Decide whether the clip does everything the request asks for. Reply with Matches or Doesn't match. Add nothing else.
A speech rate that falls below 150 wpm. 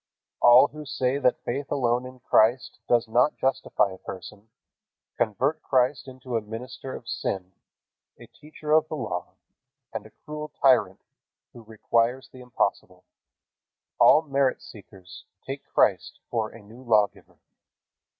Matches